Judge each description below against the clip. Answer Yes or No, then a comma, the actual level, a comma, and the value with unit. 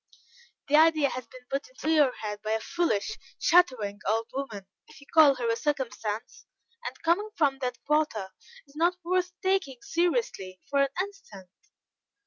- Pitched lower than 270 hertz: No, very high, 275 Hz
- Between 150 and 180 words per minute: Yes, average, 160 wpm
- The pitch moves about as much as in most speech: No, wide, 7.0 semitones